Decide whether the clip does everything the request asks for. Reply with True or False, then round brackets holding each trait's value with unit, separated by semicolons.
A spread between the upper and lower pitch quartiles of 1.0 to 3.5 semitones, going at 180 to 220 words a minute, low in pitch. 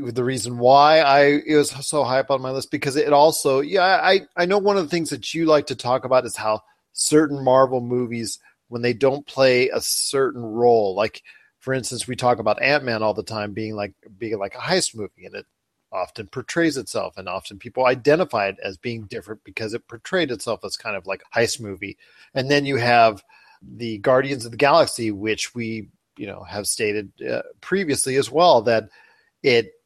False (4.3 semitones; 205 wpm; 130 Hz)